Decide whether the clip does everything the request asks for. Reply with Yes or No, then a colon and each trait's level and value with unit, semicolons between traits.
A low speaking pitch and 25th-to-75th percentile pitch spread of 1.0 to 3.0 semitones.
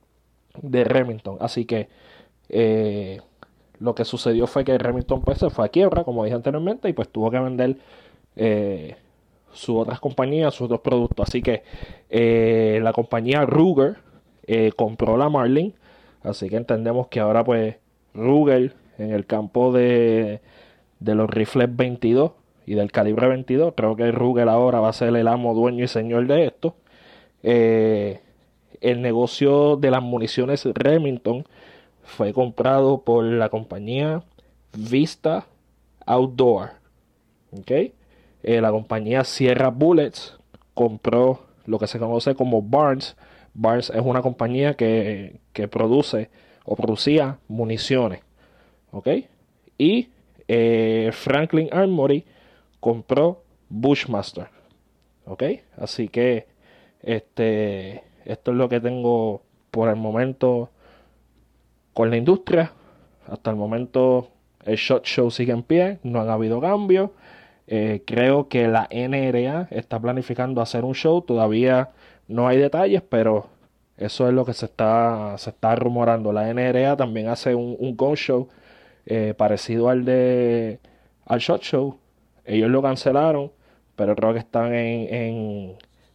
Yes: low, 120 Hz; average, 2.7 semitones